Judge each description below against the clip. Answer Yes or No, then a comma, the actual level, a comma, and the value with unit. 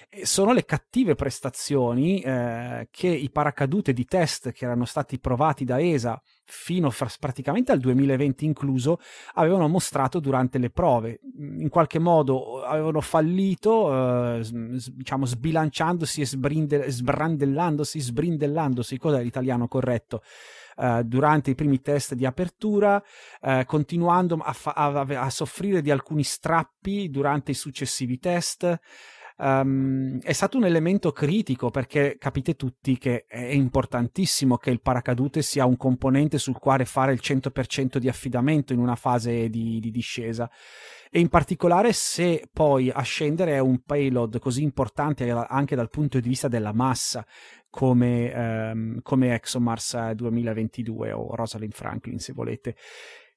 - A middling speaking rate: Yes, average, 140 wpm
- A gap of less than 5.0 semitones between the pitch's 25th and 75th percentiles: Yes, average, 3.7 semitones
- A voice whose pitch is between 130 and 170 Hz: Yes, low, 135 Hz